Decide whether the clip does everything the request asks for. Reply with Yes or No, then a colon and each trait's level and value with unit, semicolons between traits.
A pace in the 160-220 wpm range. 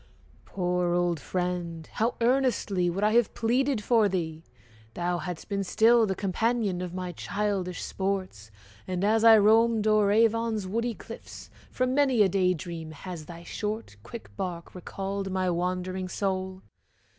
No: average, 150 wpm